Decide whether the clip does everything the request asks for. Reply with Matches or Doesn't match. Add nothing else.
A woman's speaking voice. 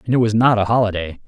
Doesn't match